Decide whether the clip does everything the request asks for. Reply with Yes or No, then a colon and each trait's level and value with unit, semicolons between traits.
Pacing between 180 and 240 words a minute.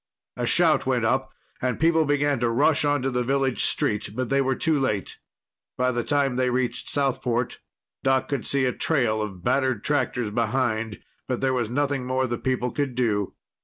Yes: average, 185 wpm